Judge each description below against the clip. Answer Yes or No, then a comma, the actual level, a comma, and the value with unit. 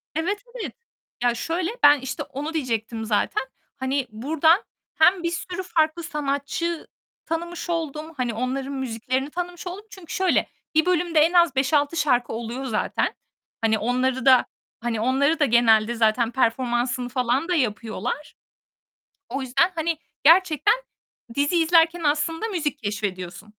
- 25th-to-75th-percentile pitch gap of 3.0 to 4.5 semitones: No, wide, 5.4 semitones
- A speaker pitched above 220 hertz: Yes, very high, 280 Hz